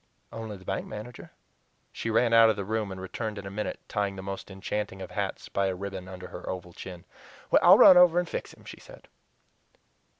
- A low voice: Yes, low, 100 Hz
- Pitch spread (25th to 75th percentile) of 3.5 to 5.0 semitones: No, average, 2.9 semitones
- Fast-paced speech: Yes, fast, 210 wpm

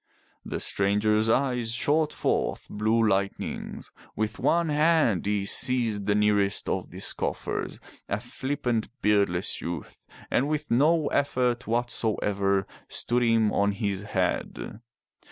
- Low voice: Yes, low, 110 Hz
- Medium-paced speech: No, slow, 120 wpm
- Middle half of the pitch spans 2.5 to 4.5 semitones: Yes, average, 3.9 semitones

